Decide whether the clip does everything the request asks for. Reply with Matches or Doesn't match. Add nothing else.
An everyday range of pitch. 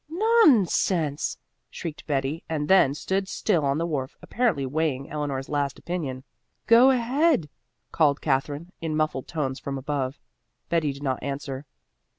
Matches